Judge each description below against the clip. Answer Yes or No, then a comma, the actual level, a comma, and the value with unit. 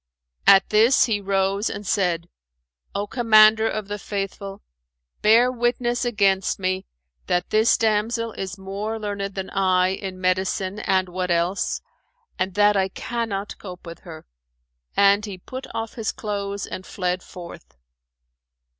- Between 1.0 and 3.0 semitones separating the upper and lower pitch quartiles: Yes, narrow, 2.5 semitones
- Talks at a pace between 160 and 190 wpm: No, average, 140 wpm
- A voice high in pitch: Yes, high, 200 Hz